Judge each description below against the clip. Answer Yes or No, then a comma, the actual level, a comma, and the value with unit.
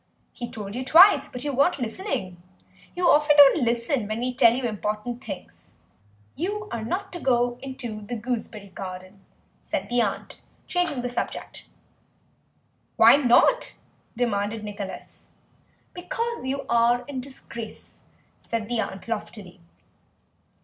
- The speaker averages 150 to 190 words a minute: No, slow, 135 wpm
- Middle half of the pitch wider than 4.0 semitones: Yes, average, 4.6 semitones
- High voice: Yes, high, 240 Hz